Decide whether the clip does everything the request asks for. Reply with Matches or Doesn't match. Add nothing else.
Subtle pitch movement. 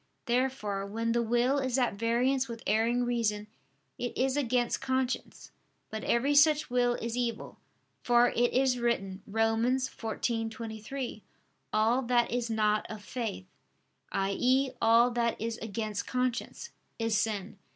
Matches